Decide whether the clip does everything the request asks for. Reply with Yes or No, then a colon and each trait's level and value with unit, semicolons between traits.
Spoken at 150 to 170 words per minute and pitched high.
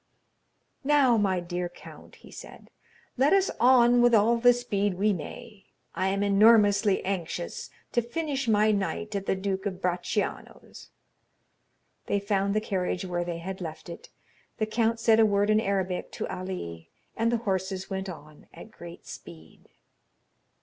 Yes: average, 155 wpm; high, 200 Hz